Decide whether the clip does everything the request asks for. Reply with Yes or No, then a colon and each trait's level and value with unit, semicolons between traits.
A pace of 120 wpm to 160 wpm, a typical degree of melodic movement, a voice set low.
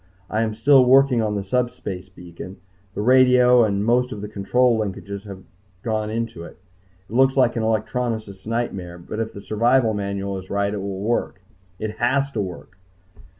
No: average, 180 wpm; average, 3.7 semitones; low, 110 Hz